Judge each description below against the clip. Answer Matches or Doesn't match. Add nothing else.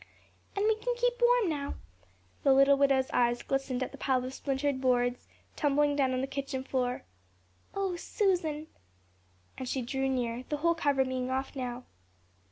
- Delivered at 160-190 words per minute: Matches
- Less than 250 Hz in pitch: Doesn't match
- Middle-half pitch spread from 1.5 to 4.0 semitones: Matches